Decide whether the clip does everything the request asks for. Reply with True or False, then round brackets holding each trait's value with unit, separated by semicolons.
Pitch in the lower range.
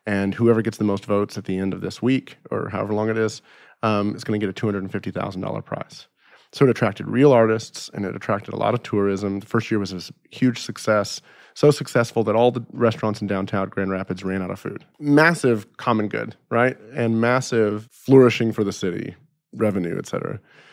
True (110 Hz)